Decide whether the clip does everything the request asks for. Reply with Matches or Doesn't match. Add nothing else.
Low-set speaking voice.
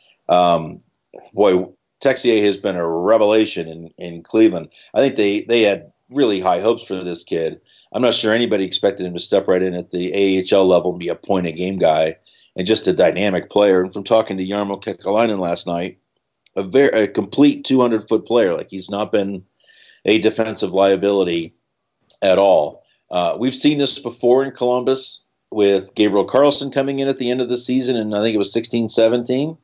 Matches